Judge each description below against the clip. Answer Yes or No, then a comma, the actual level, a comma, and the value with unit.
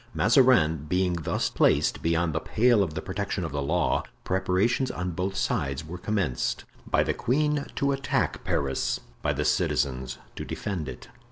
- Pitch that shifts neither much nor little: No, wide, 5.8 semitones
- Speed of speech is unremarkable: Yes, average, 160 wpm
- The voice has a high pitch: No, very low, 90 Hz